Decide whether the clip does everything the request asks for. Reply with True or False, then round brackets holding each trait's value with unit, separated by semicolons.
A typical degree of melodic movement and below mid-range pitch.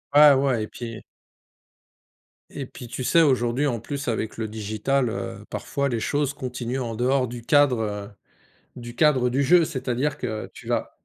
True (3.2 semitones; 125 Hz)